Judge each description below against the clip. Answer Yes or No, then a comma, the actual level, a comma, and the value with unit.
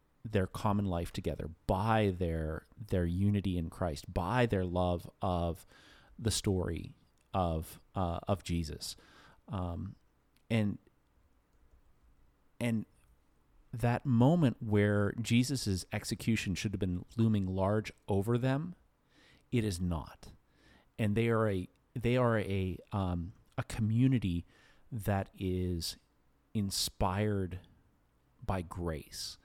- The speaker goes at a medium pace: No, slow, 110 wpm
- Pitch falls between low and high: No, low, 100 Hz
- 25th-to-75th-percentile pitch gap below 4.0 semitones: No, average, 4.3 semitones